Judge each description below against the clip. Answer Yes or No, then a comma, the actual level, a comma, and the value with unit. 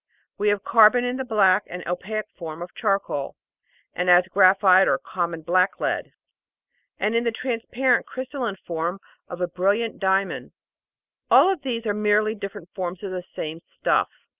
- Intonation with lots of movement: No, average, 3.8 semitones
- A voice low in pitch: No, high, 195 Hz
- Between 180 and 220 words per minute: No, average, 165 wpm